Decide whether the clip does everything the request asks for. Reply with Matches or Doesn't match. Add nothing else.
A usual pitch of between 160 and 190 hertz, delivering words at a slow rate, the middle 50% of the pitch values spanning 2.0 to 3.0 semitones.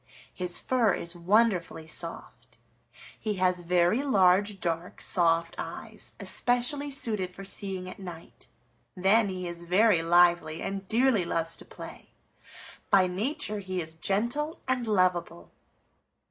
Doesn't match